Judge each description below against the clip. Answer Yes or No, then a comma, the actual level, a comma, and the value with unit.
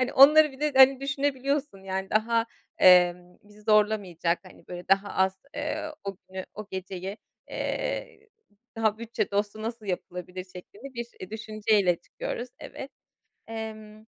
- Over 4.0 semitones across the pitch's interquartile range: Yes, average, 5.3 semitones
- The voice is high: Yes, high, 215 Hz